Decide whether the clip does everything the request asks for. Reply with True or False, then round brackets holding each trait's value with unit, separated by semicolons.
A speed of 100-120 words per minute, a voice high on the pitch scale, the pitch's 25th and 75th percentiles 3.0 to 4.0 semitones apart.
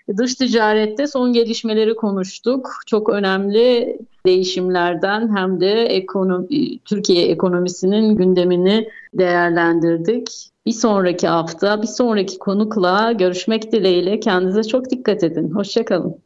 True (105 wpm; 205 Hz; 3.7 semitones)